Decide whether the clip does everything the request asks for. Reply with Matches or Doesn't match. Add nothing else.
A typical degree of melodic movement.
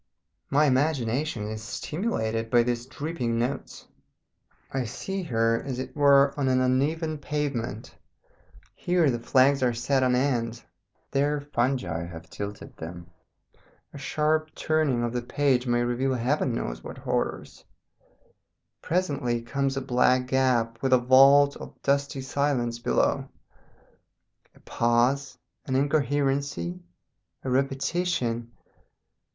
Matches